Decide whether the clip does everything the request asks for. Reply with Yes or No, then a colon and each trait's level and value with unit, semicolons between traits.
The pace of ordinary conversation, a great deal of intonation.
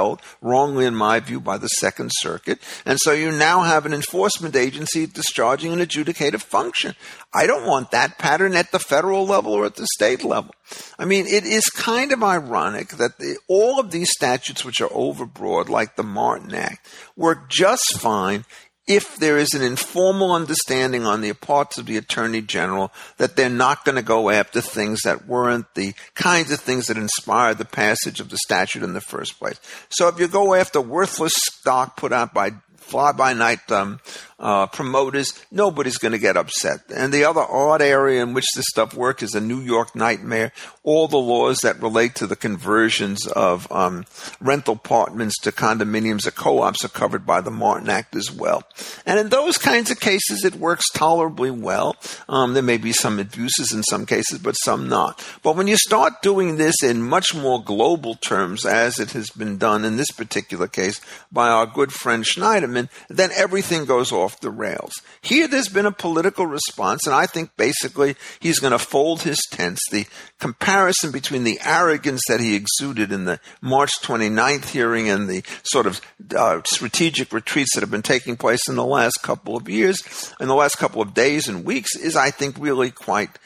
Yes: average, 195 wpm; wide, 7.1 semitones